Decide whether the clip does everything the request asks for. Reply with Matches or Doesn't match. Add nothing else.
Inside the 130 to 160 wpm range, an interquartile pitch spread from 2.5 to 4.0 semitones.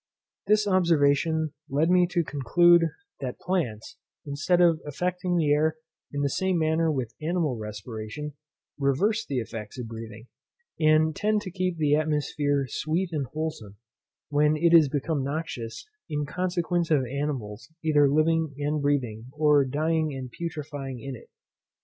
Matches